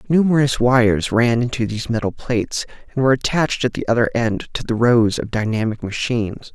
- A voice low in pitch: Yes, low, 120 Hz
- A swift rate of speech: No, average, 185 wpm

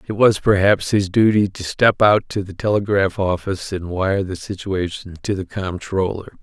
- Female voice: No, male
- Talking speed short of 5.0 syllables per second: Yes, 4.7 syllables/s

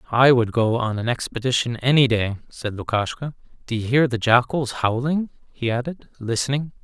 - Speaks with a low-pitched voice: Yes, low, 125 Hz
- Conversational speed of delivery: Yes, average, 160 wpm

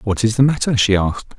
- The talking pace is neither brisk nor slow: No, fast, 260 wpm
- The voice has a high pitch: No, low, 110 Hz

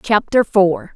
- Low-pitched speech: No, high, 210 Hz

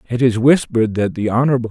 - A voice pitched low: Yes, low, 120 Hz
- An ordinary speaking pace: No, fast, 210 wpm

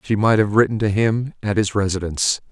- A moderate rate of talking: No, fast, 215 wpm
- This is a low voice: Yes, low, 105 Hz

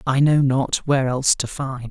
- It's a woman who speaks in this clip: No, male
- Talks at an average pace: No, fast, 220 wpm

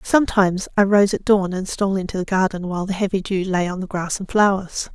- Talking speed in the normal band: No, fast, 245 wpm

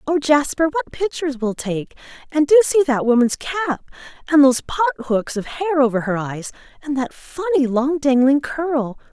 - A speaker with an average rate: Yes, average, 170 wpm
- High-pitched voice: Yes, very high, 285 Hz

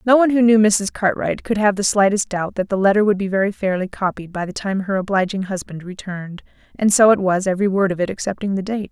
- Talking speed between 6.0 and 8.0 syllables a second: Yes, 6.3 syllables/s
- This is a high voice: Yes, high, 195 Hz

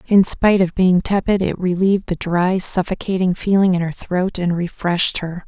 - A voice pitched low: No, medium, 185 Hz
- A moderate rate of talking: Yes, average, 185 wpm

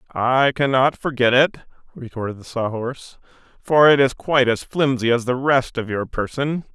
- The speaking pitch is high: No, low, 130 Hz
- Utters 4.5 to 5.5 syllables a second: Yes, 4.9 syllables/s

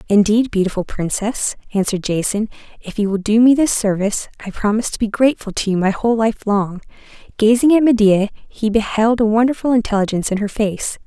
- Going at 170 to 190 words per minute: Yes, average, 185 wpm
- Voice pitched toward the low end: No, high, 215 Hz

